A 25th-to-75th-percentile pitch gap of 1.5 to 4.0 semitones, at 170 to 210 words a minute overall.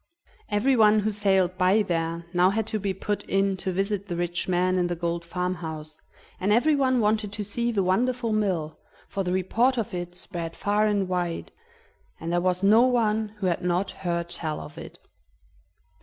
Yes: average, 3.3 semitones; average, 185 wpm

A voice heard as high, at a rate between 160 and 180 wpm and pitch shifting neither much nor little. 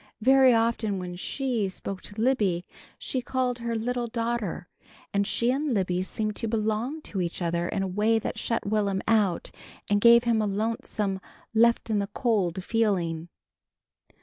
Yes: high, 215 Hz; average, 165 wpm; average, 3.4 semitones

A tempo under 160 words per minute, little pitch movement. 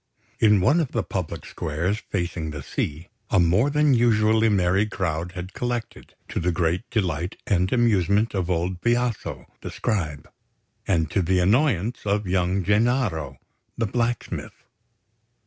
No: average, 145 wpm; average, 4.5 semitones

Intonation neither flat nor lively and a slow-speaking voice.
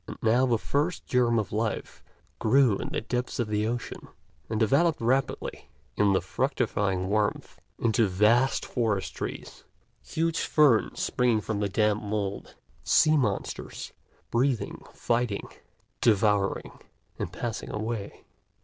Yes: average, 3.1 semitones; slow, 130 wpm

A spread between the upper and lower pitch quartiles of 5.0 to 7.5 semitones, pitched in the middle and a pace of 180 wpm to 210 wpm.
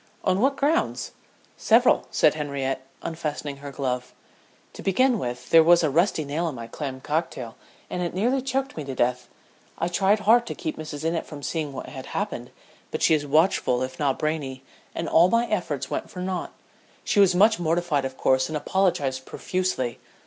Yes: wide, 5.6 semitones; medium, 155 Hz; average, 185 wpm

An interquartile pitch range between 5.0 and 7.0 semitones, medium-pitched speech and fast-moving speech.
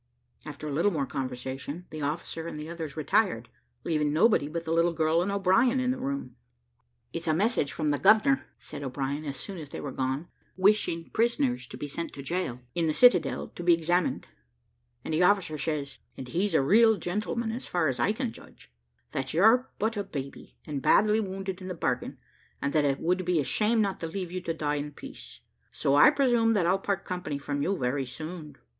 Yes: wide, 5.6 semitones; medium, 165 Hz; fast, 215 wpm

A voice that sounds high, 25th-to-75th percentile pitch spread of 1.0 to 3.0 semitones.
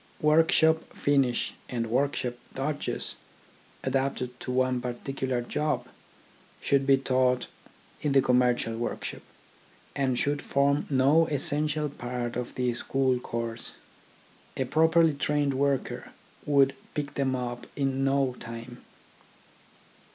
No: low, 135 Hz; narrow, 2.4 semitones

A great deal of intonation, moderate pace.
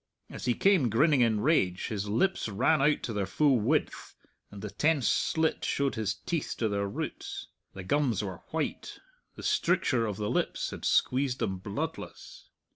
Yes: wide, 6.1 semitones; average, 175 wpm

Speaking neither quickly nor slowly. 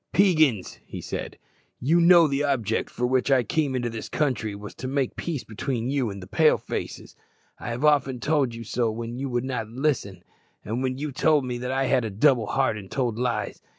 No: fast, 215 wpm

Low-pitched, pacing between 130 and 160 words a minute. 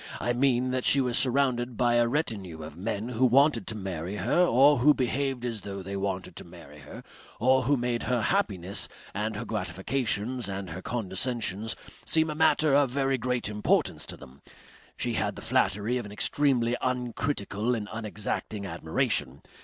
No: low, 120 Hz; average, 175 wpm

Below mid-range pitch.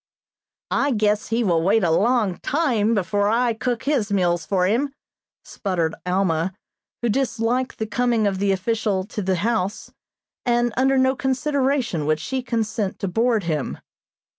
No: high, 220 Hz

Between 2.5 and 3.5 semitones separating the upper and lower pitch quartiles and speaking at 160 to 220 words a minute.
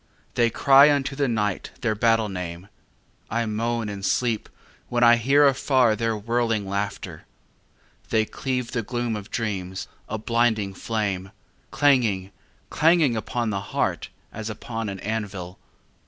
No: average, 2.9 semitones; average, 140 wpm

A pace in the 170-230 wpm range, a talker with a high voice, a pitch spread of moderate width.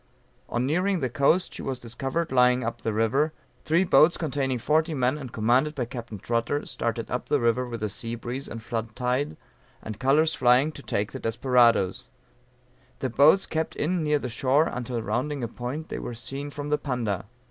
No: average, 190 wpm; low, 130 Hz; average, 4.0 semitones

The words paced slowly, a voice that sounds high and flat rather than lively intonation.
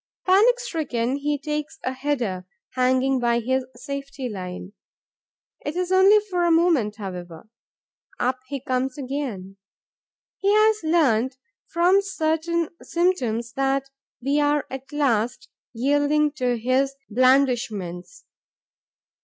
No: slow, 115 wpm; very high, 270 Hz; average, 4.6 semitones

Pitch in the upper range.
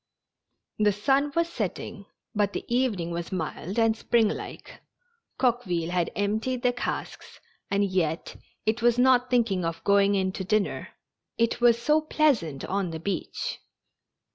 Yes: high, 210 Hz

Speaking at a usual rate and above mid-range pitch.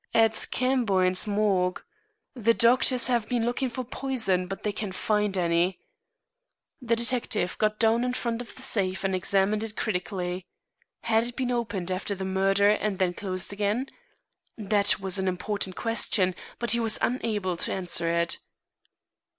Yes: average, 160 wpm; high, 210 Hz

